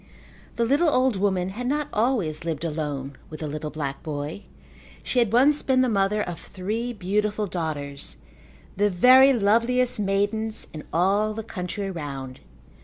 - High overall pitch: Yes, high, 200 Hz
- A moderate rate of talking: Yes, average, 155 wpm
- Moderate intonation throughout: No, wide, 6.6 semitones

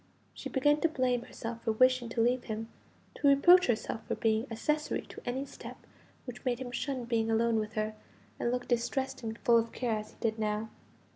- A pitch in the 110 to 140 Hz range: No, high, 240 Hz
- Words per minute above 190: Yes, fast, 205 wpm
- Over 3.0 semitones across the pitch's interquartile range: No, narrow, 2.4 semitones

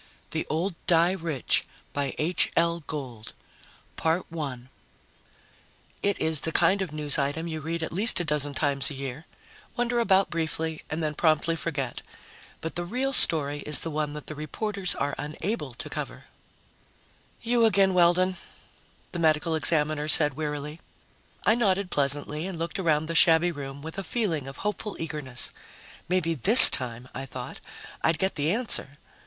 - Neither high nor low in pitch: Yes, medium, 160 Hz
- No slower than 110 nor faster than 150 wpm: No, average, 165 wpm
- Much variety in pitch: No, average, 3.6 semitones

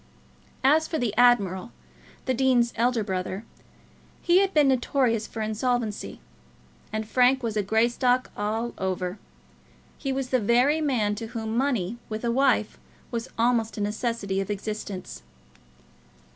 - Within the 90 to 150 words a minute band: Yes, average, 140 wpm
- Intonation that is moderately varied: Yes, average, 3.3 semitones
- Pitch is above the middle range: Yes, high, 230 Hz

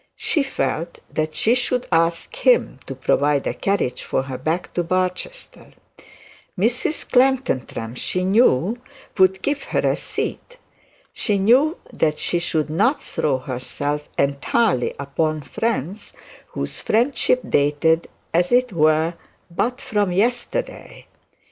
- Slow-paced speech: Yes, slow, 125 wpm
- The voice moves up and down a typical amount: No, wide, 8.2 semitones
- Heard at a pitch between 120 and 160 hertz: No, medium, 175 Hz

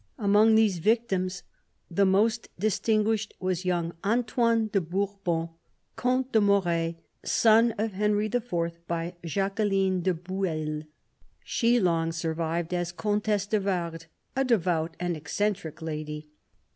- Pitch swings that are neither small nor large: Yes, average, 4.2 semitones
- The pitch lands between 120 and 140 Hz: No, high, 190 Hz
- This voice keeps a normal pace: No, slow, 120 wpm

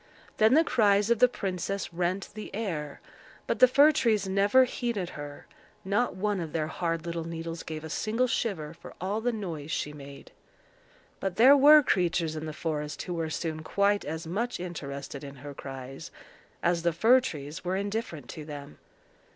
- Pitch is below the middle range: No, medium, 175 Hz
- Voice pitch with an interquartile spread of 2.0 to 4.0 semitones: No, wide, 5.5 semitones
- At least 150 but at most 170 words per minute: No, average, 180 wpm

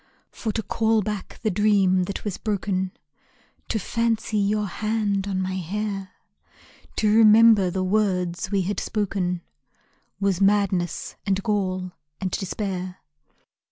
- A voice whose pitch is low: No, high, 200 Hz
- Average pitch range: No, narrow, 2.3 semitones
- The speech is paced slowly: Yes, slow, 125 wpm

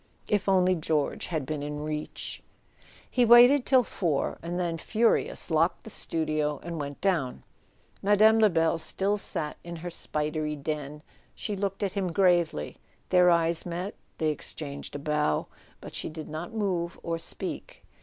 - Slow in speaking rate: No, average, 155 wpm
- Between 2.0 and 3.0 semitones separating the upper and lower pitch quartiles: No, average, 4.2 semitones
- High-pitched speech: No, medium, 170 Hz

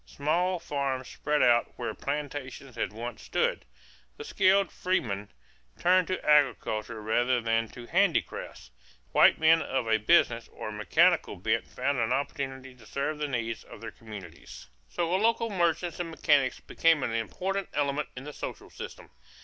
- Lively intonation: Yes, wide, 6.2 semitones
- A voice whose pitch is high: No, medium, 140 Hz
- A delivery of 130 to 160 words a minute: Yes, average, 155 wpm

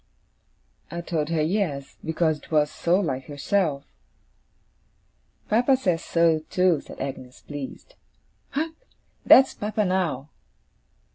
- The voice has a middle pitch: Yes, medium, 165 Hz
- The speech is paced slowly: Yes, slow, 115 wpm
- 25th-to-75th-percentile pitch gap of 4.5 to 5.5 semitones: Yes, average, 5.1 semitones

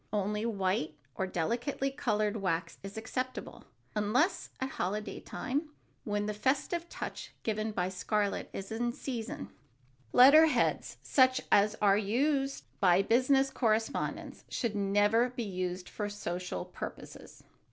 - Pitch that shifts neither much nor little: Yes, average, 4.5 semitones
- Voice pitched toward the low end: No, high, 215 Hz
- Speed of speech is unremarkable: No, slow, 130 wpm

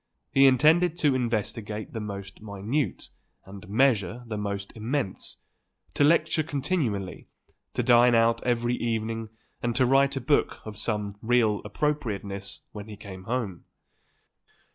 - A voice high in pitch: No, low, 115 Hz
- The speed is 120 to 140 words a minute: Yes, slow, 135 wpm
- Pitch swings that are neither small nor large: Yes, average, 4.4 semitones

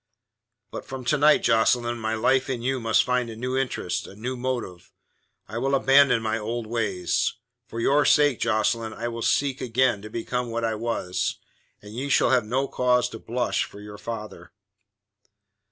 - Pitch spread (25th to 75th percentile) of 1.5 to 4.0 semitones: Yes, narrow, 2.5 semitones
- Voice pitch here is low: Yes, low, 120 Hz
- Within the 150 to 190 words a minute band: Yes, average, 180 wpm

